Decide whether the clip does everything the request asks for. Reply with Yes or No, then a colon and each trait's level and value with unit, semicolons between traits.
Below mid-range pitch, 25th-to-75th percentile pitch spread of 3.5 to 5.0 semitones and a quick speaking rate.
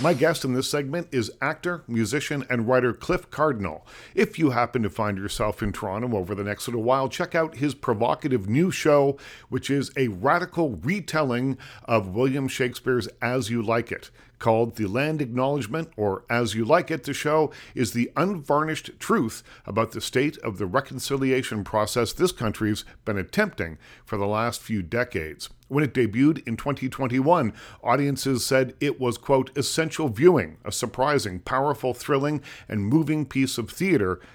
No: low, 130 Hz; average, 4.5 semitones; average, 165 wpm